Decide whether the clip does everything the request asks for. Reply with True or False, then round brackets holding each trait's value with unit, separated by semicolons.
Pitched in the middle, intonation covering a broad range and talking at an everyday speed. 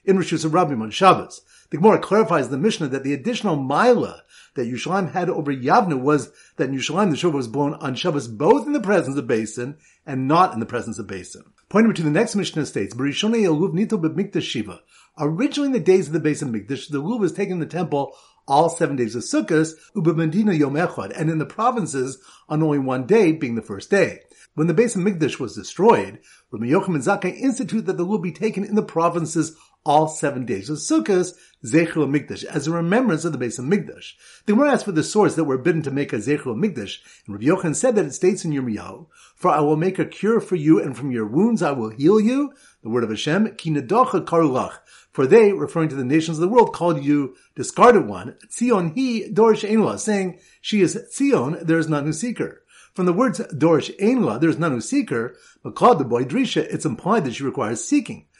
False (165 Hz; 6.2 semitones; 215 wpm)